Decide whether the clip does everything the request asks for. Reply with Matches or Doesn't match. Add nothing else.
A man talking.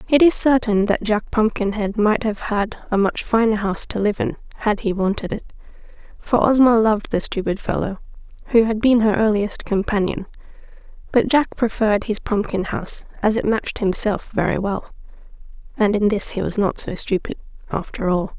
Doesn't match